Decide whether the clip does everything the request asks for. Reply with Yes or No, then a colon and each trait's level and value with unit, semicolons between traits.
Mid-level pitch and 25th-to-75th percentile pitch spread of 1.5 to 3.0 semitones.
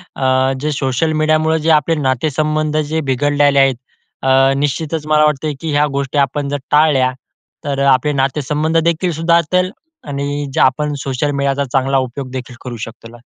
Yes: medium, 145 Hz; narrow, 2.4 semitones